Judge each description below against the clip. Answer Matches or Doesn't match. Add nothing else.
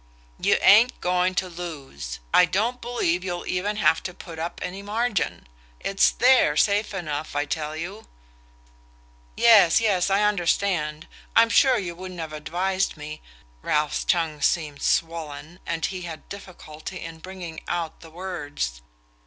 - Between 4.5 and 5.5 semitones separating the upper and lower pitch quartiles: Doesn't match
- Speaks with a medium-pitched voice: Matches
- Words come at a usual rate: Matches